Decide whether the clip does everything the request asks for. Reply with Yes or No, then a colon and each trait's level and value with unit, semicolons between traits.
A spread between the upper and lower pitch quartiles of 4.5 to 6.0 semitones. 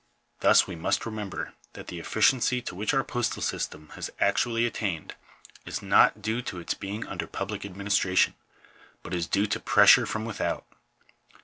No: average, 3.8 semitones